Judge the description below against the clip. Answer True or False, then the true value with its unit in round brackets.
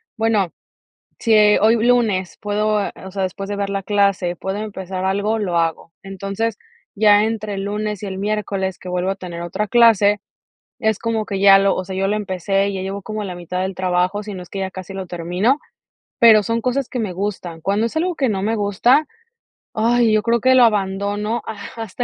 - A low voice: False (200 Hz)